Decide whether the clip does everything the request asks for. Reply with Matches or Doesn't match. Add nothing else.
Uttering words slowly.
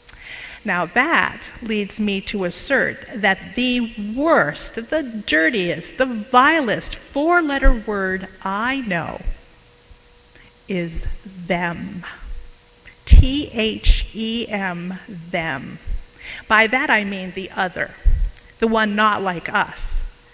Matches